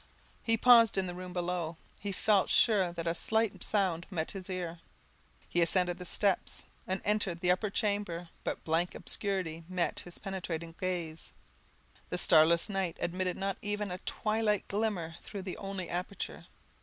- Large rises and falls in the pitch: No, average, 2.7 semitones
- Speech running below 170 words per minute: Yes, average, 160 wpm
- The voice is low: No, medium, 185 Hz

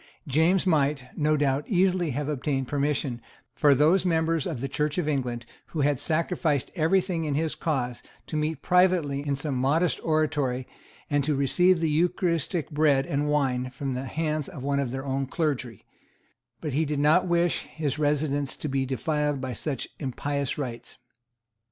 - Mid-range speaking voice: Yes, medium, 150 Hz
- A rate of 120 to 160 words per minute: No, average, 170 wpm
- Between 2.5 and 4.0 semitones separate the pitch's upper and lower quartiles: Yes, average, 2.9 semitones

